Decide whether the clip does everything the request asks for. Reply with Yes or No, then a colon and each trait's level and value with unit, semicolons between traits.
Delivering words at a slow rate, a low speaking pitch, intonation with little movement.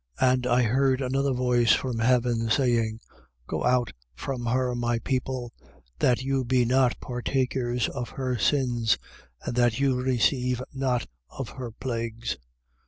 No: average, 145 wpm; low, 125 Hz; narrow, 1.5 semitones